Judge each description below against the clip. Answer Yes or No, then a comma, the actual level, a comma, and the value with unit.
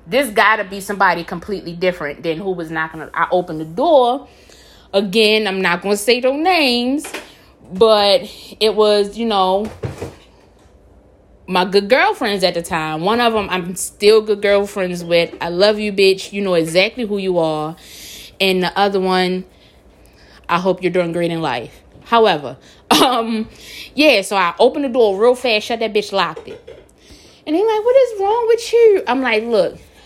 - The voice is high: Yes, high, 205 Hz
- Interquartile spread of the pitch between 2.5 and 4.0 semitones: No, average, 4.7 semitones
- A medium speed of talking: Yes, average, 175 wpm